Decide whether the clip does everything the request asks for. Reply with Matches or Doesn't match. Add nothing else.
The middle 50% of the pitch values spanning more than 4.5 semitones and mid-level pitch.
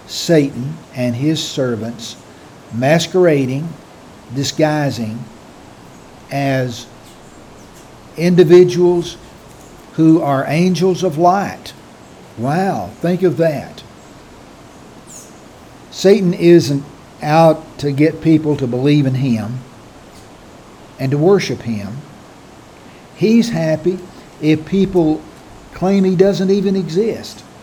Matches